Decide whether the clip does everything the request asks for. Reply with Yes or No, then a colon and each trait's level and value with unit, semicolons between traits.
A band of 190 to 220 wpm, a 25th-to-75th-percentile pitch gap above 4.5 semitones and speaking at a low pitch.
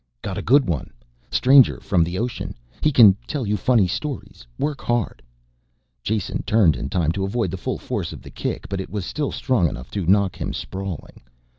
Yes: average, 195 wpm; wide, 5.5 semitones; low, 100 Hz